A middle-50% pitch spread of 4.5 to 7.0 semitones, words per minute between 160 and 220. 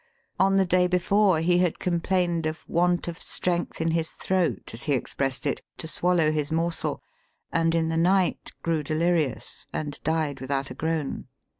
No: narrow, 2.4 semitones; average, 170 wpm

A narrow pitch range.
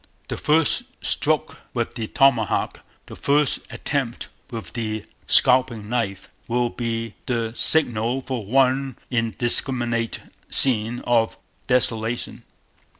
Yes: narrow, 2.3 semitones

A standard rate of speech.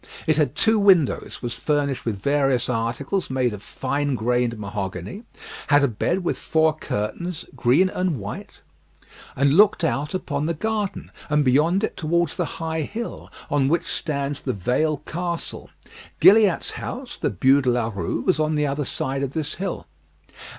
Yes: average, 165 wpm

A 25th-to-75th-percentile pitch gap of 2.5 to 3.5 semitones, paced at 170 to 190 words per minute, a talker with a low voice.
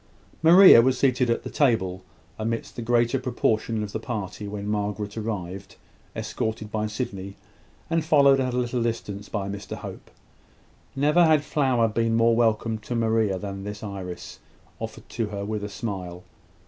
No: average, 3.1 semitones; average, 160 wpm; low, 110 Hz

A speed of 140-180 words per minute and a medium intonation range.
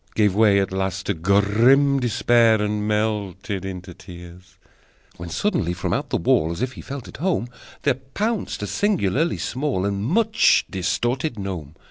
No: average, 160 wpm; wide, 5.8 semitones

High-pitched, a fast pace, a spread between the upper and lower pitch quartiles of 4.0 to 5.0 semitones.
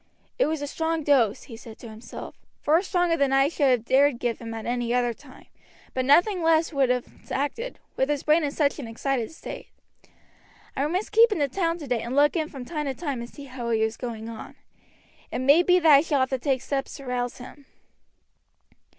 Yes: very high, 275 Hz; fast, 220 wpm; average, 4.3 semitones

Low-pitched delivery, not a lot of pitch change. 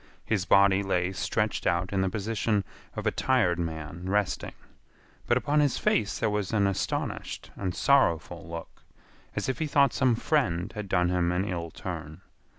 No: very low, 95 Hz; average, 4.3 semitones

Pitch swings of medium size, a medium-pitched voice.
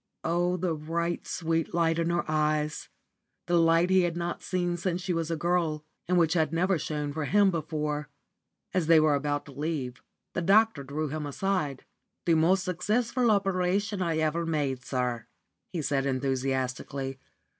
Yes: average, 3.2 semitones; medium, 165 Hz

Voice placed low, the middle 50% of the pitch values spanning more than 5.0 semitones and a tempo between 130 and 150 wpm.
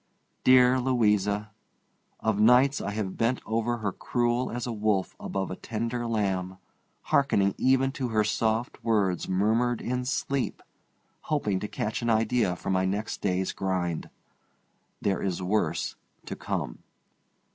No: low, 110 Hz; average, 4.0 semitones; average, 140 wpm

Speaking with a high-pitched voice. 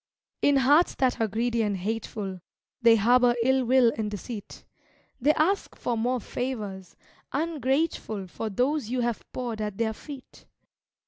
Yes: high, 240 Hz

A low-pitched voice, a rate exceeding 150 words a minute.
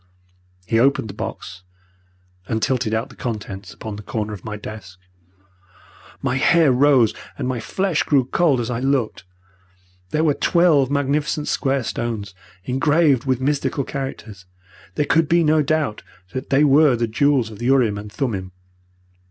Yes: low, 130 Hz; average, 160 wpm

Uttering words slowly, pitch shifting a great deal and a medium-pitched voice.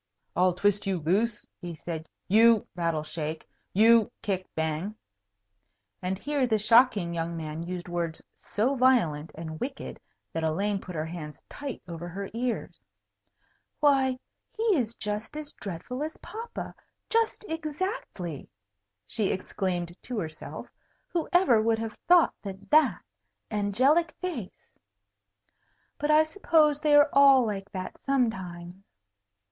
No: slow, 130 wpm; wide, 7.8 semitones; high, 205 Hz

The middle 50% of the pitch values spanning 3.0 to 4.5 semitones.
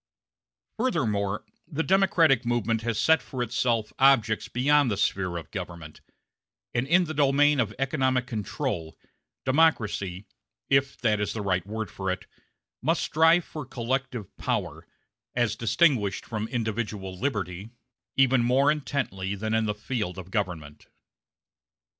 No: average, 5.2 semitones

